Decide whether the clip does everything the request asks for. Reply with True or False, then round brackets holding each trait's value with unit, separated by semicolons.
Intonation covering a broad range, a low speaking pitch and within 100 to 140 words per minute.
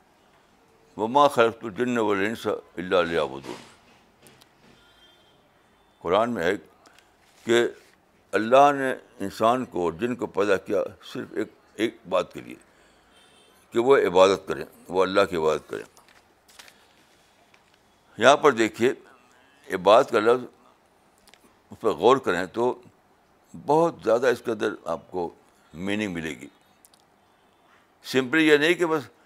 True (6.7 semitones; 125 Hz; 125 wpm)